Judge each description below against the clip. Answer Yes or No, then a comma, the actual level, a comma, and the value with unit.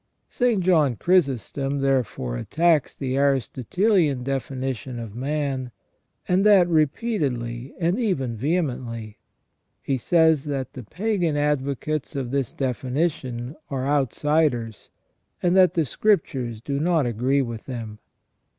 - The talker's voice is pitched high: No, medium, 140 Hz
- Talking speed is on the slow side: Yes, slow, 120 wpm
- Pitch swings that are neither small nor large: Yes, average, 4.6 semitones